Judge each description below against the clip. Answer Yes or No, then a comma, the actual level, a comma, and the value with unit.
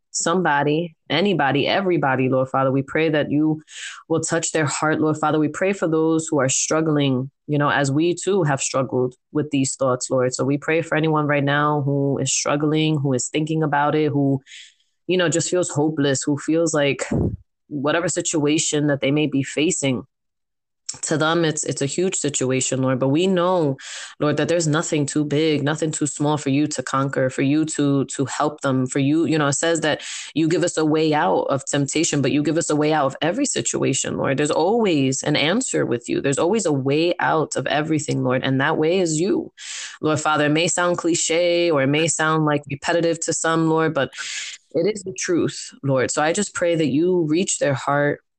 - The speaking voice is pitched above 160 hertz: No, medium, 150 Hz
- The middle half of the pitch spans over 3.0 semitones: No, average, 2.7 semitones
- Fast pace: Yes, fast, 210 wpm